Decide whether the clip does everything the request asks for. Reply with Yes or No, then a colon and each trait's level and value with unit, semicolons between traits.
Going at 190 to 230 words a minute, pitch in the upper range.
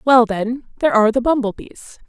Yes: average, 200 wpm; high, 240 Hz